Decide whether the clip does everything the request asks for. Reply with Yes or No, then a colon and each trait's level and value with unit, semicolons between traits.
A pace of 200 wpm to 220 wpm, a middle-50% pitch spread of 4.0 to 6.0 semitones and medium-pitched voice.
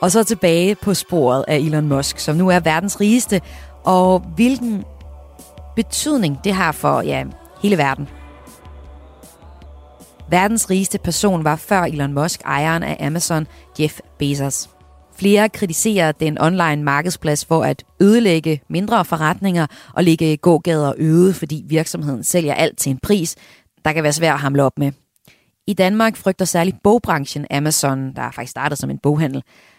No: average, 155 wpm; average, 5.0 semitones; medium, 160 Hz